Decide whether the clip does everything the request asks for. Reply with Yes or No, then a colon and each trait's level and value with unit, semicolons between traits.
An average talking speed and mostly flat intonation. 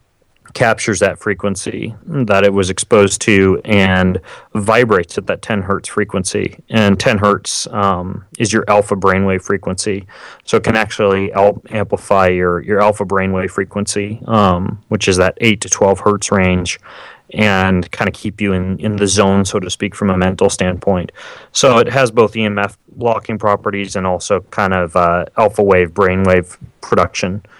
Yes: average, 165 wpm; narrow, 1.9 semitones